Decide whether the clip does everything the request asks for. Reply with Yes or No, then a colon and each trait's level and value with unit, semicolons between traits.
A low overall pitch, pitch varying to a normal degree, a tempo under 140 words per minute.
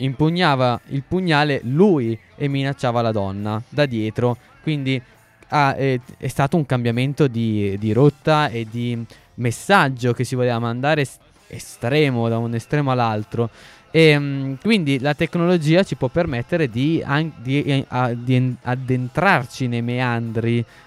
Yes: low, 130 Hz; average, 3.9 semitones; average, 130 wpm